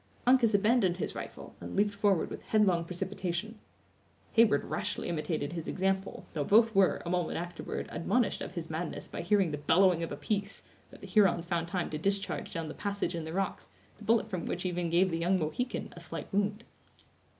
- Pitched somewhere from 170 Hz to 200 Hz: Yes, medium, 185 Hz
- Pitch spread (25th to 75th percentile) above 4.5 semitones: No, average, 3.3 semitones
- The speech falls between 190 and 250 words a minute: Yes, average, 195 wpm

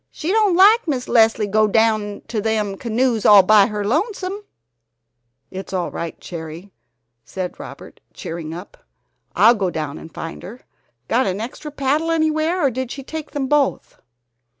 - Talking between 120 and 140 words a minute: No, average, 160 wpm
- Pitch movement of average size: No, wide, 7.1 semitones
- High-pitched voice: Yes, high, 225 Hz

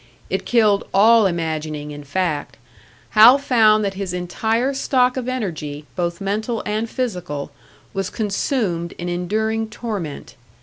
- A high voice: Yes, high, 200 Hz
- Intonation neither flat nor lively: Yes, average, 4.8 semitones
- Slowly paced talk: Yes, slow, 130 wpm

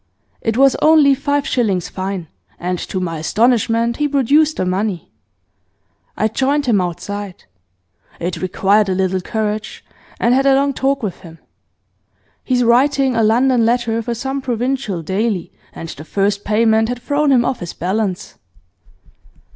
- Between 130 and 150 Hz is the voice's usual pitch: No, high, 225 Hz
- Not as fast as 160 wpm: Yes, average, 150 wpm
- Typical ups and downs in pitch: No, wide, 5.7 semitones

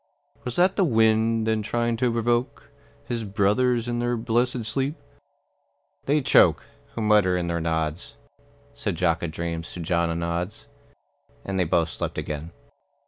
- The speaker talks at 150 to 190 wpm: Yes, average, 155 wpm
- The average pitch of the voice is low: Yes, low, 110 Hz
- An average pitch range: No, wide, 5.8 semitones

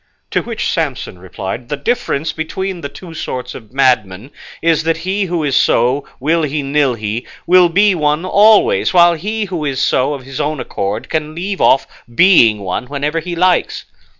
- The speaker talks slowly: No, average, 180 wpm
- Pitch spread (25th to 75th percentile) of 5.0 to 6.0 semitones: Yes, wide, 5.5 semitones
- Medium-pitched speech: Yes, medium, 150 Hz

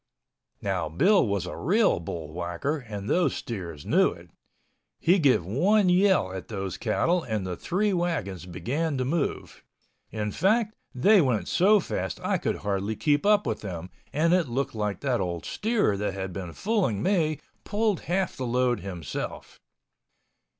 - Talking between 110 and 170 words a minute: Yes, average, 160 wpm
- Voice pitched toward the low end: Yes, low, 125 Hz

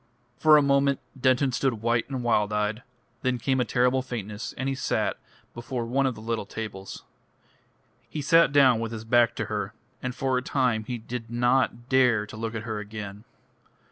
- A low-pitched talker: Yes, low, 120 Hz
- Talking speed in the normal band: Yes, average, 190 wpm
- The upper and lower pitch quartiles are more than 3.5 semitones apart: No, average, 3.0 semitones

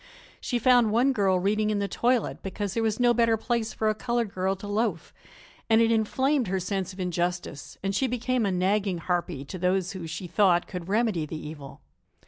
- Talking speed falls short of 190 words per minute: No, fast, 205 wpm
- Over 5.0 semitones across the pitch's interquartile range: No, average, 3.9 semitones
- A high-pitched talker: Yes, high, 200 Hz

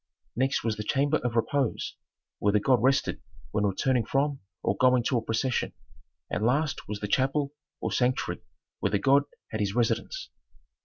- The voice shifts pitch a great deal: No, average, 3.9 semitones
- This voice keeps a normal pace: Yes, average, 170 wpm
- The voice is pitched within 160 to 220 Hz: No, low, 125 Hz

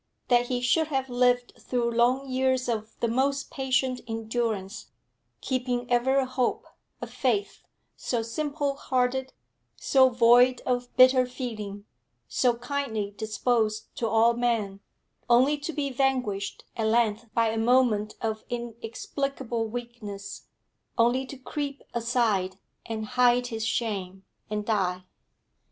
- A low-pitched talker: No, high, 240 Hz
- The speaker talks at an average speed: No, slow, 130 wpm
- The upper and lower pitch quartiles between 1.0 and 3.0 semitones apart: Yes, narrow, 2.6 semitones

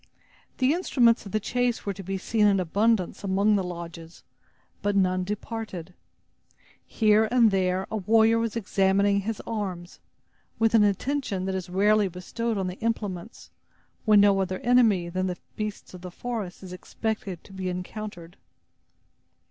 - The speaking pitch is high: Yes, high, 200 Hz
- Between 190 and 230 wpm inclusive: No, average, 155 wpm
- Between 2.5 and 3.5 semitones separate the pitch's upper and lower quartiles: Yes, average, 3.2 semitones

